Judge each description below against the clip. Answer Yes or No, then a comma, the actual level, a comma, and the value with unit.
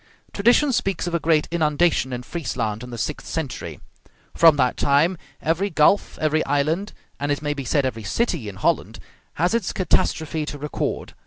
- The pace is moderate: Yes, average, 175 wpm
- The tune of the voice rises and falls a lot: No, average, 4.4 semitones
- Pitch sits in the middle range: Yes, medium, 150 Hz